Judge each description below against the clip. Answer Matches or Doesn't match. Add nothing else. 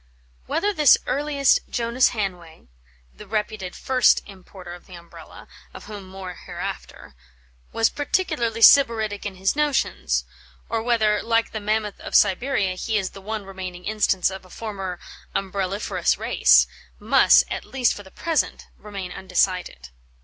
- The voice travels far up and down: Doesn't match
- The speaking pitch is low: Doesn't match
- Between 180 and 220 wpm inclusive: Doesn't match